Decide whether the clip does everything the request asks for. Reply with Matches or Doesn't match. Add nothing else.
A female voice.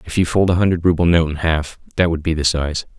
Doesn't match